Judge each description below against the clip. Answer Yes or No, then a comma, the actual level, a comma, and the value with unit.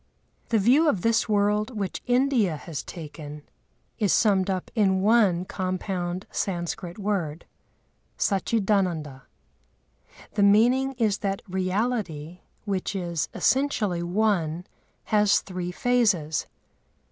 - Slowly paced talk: Yes, slow, 105 wpm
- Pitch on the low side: No, high, 195 Hz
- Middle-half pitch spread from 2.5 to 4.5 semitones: Yes, average, 3.8 semitones